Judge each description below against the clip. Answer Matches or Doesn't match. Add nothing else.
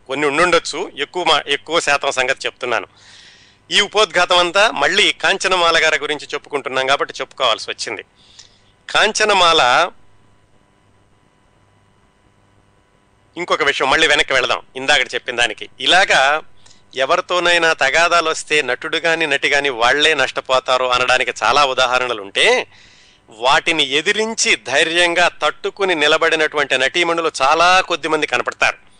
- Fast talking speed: Doesn't match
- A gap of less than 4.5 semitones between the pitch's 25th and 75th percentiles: Doesn't match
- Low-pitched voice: Doesn't match